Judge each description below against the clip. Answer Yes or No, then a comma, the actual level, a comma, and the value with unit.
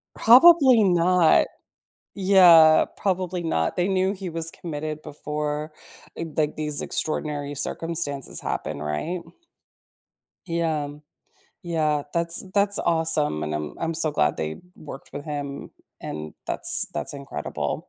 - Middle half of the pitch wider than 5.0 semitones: No, average, 3.4 semitones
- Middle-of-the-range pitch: Yes, medium, 160 Hz